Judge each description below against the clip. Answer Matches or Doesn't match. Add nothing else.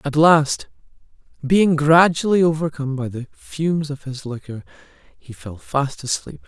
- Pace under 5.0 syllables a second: Matches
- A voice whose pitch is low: Doesn't match